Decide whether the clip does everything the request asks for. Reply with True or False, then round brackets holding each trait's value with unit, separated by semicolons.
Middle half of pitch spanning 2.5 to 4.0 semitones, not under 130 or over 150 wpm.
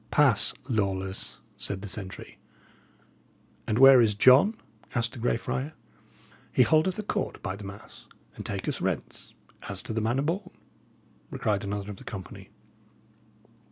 False (5.2 semitones; 145 wpm)